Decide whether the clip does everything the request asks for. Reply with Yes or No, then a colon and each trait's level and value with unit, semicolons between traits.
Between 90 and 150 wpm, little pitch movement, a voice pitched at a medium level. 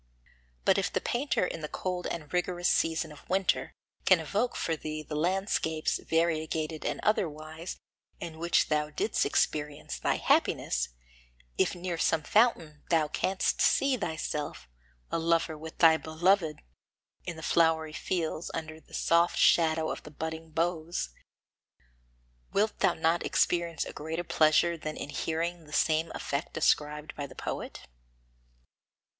Yes: average, 145 wpm; narrow, 2.0 semitones; medium, 160 Hz